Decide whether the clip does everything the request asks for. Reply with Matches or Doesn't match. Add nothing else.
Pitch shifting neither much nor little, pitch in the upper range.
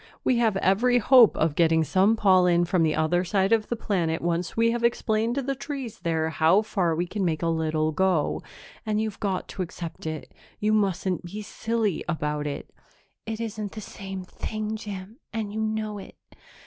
Matches